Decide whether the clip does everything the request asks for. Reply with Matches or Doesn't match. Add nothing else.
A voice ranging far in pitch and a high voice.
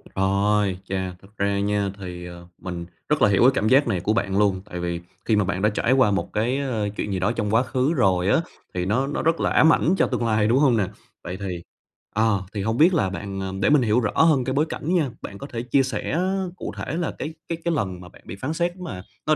Doesn't match